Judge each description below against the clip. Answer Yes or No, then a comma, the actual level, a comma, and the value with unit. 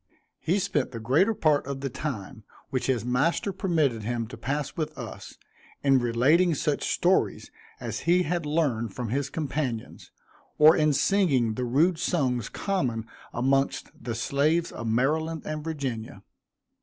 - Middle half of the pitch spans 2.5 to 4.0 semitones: No, average, 4.7 semitones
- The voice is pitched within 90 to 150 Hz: Yes, medium, 140 Hz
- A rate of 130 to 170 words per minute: Yes, average, 150 wpm